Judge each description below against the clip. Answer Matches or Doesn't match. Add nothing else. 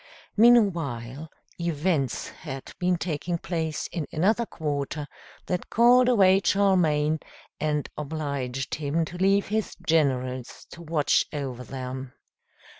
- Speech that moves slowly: Matches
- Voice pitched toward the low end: Doesn't match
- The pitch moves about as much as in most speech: Matches